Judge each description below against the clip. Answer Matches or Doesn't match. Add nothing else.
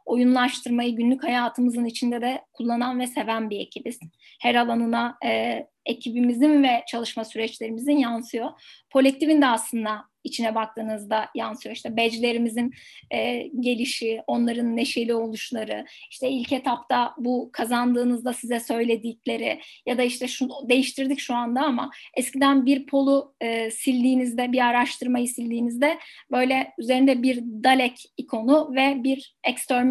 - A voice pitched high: Matches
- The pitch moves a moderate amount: Doesn't match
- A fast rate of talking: Doesn't match